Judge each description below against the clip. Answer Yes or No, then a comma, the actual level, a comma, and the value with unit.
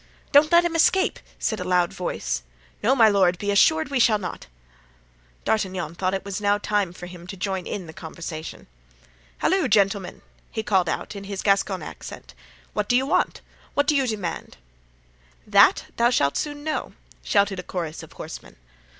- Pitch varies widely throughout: No, average, 4.9 semitones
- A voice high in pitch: Yes, high, 200 Hz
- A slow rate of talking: No, average, 175 wpm